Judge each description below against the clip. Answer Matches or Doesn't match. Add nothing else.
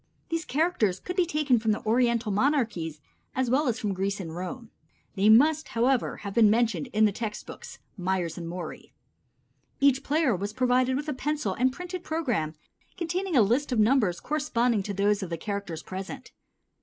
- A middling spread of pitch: Doesn't match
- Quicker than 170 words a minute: Matches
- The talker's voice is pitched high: Matches